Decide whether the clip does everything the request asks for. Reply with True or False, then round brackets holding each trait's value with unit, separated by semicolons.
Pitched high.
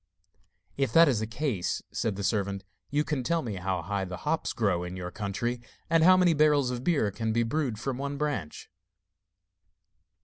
False (120 Hz)